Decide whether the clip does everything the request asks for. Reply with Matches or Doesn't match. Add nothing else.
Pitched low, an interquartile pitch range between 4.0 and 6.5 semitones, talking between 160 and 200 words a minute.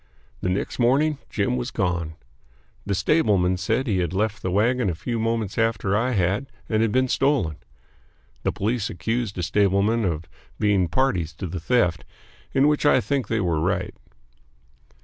Matches